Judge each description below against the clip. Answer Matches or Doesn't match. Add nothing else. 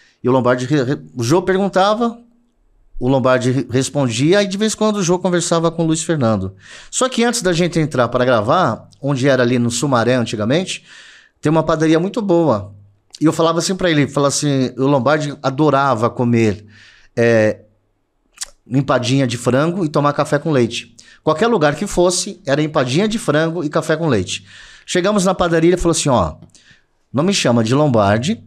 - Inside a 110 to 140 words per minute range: Doesn't match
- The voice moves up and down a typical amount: Doesn't match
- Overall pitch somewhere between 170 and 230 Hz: Doesn't match